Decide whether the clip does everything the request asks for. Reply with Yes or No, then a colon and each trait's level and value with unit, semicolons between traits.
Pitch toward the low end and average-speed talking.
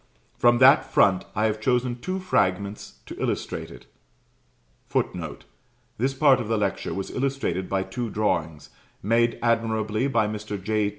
Yes: low, 110 Hz; average, 145 wpm